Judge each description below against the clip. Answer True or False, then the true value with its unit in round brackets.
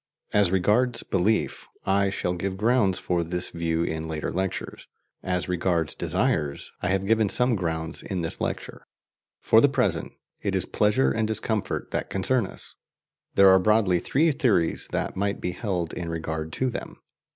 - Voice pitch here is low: True (95 Hz)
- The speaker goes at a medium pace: True (165 wpm)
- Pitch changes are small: False (3.9 semitones)